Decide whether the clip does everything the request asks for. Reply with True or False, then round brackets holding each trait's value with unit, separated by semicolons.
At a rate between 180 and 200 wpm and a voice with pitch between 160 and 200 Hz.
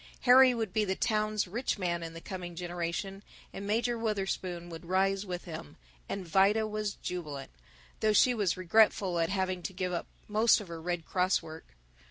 True (185 wpm; 190 Hz)